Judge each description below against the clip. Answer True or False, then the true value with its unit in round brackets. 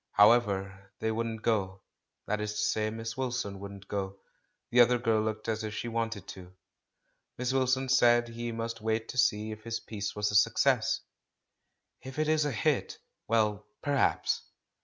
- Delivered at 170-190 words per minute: True (180 wpm)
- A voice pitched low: True (110 Hz)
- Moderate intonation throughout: False (2.3 semitones)